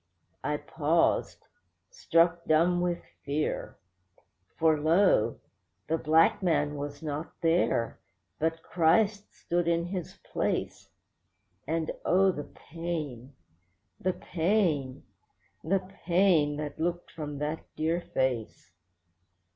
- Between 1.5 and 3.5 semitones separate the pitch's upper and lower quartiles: Yes, average, 2.9 semitones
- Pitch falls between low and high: Yes, medium, 165 Hz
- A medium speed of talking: No, slow, 105 wpm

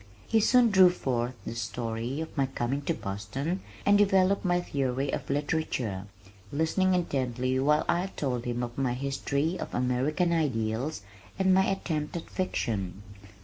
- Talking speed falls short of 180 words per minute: Yes, average, 150 wpm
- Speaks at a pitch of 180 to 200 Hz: No, medium, 140 Hz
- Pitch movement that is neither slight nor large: No, wide, 6.4 semitones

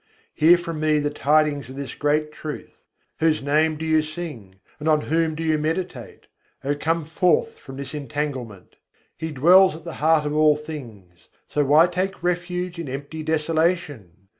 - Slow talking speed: No, average, 170 wpm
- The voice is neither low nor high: Yes, medium, 155 Hz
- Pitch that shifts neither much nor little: No, narrow, 2.2 semitones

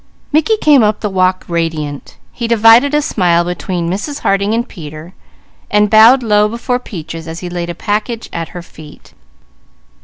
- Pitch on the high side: Yes, high, 200 Hz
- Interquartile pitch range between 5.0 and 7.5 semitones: Yes, average, 5.3 semitones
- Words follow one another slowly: No, average, 165 wpm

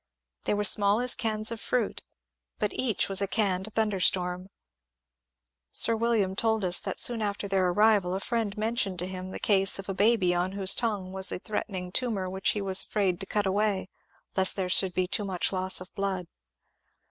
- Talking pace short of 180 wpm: No, average, 195 wpm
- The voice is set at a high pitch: Yes, high, 195 Hz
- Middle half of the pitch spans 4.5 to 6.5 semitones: No, narrow, 2.5 semitones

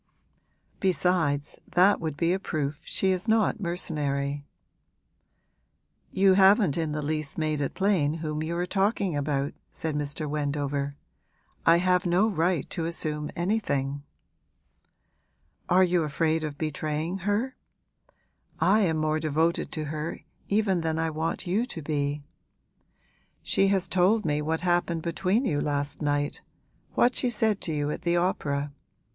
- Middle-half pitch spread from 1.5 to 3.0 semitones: No, average, 3.9 semitones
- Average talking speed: Yes, average, 145 wpm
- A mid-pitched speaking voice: Yes, medium, 160 Hz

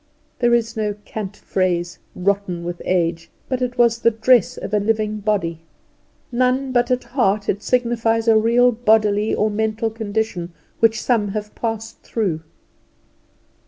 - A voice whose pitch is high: Yes, high, 220 Hz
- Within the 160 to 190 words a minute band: No, average, 150 wpm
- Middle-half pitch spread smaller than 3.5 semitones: Yes, average, 2.7 semitones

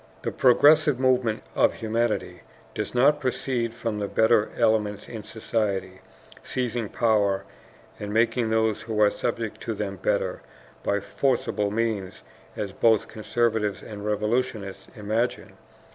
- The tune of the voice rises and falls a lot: No, narrow, 2.4 semitones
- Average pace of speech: No, slow, 130 wpm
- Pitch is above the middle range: No, low, 110 Hz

